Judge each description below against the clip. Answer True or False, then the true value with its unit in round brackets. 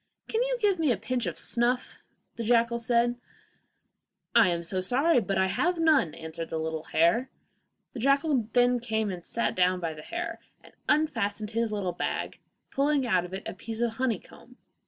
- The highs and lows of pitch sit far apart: True (5.9 semitones)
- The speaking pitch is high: True (235 Hz)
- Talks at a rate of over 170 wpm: True (190 wpm)